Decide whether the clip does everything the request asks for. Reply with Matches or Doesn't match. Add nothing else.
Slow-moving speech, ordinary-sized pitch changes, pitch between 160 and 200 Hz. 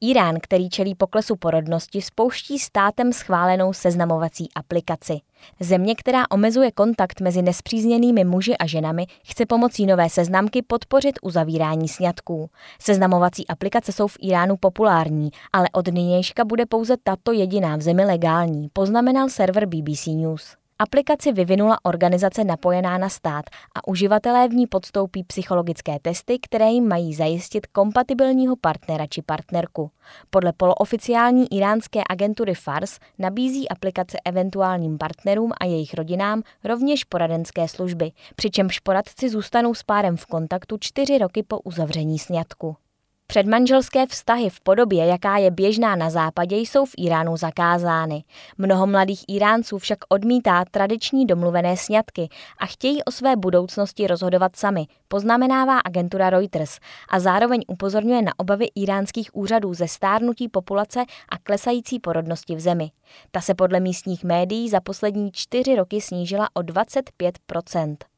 Doesn't match